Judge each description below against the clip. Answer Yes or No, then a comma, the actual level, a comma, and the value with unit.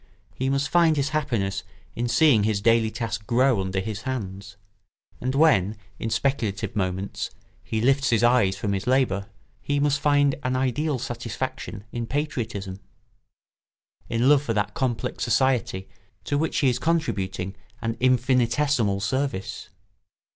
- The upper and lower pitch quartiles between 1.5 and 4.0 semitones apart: No, average, 5.2 semitones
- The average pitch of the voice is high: No, low, 120 Hz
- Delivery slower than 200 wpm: Yes, average, 140 wpm